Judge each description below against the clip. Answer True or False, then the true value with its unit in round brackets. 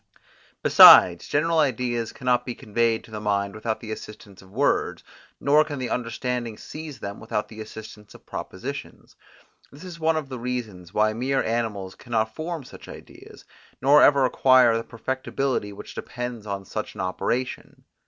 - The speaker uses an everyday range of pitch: True (3.6 semitones)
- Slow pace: False (165 wpm)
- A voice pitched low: True (120 Hz)